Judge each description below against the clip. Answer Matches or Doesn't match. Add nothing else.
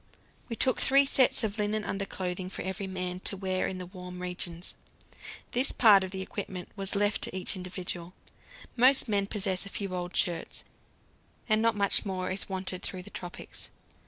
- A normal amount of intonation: Doesn't match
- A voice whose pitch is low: Doesn't match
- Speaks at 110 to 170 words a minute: Doesn't match